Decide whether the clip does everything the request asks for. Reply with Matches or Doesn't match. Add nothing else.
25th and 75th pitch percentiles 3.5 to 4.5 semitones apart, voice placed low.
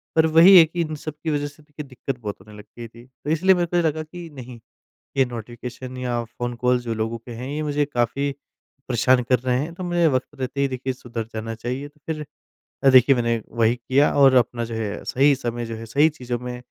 Matches